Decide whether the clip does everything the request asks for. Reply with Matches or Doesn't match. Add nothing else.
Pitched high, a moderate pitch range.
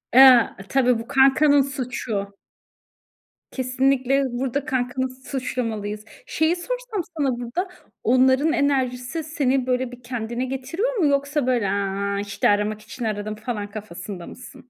Matches